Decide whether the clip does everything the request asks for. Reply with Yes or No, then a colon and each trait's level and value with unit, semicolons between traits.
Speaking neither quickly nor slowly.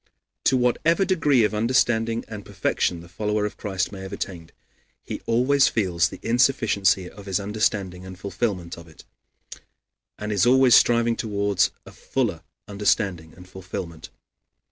Yes: average, 145 wpm